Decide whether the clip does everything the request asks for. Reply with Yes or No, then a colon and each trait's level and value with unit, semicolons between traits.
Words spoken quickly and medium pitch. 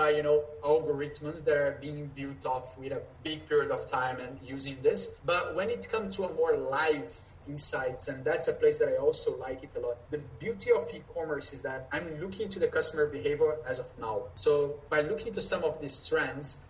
Yes: fast, 220 wpm; medium, 155 Hz